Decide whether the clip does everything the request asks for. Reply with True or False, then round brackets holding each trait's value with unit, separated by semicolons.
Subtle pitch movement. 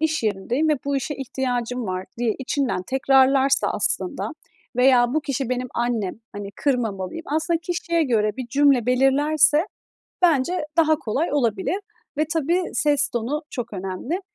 False (4.2 semitones)